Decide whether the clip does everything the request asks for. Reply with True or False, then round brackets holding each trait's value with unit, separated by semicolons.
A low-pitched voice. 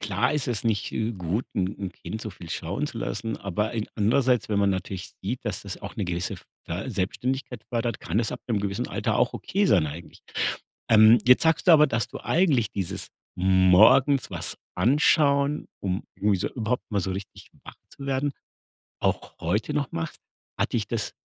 True (110 Hz)